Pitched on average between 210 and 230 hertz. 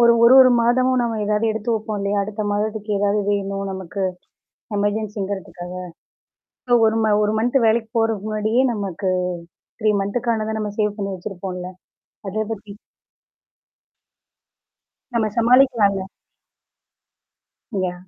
Yes: high, 215 Hz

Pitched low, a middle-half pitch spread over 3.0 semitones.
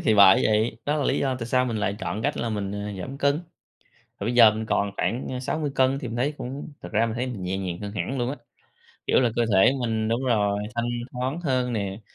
Yes: low, 120 Hz; average, 3.8 semitones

